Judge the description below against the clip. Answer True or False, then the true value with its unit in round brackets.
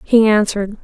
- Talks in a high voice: True (210 Hz)